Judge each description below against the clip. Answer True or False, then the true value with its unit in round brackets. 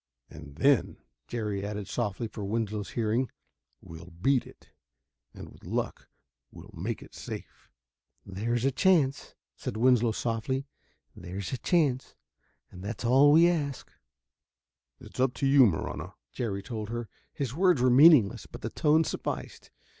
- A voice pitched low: True (120 Hz)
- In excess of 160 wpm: False (145 wpm)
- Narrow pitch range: False (4.6 semitones)